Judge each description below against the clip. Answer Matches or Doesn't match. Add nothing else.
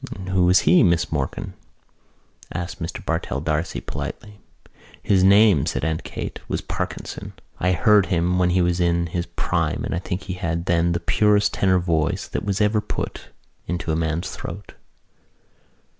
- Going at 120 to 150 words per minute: Doesn't match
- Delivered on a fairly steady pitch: Matches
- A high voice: Doesn't match